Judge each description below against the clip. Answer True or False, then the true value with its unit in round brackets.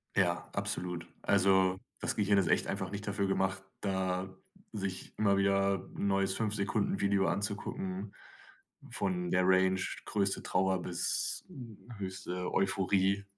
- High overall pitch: False (95 Hz)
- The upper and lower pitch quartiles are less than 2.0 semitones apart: True (1.3 semitones)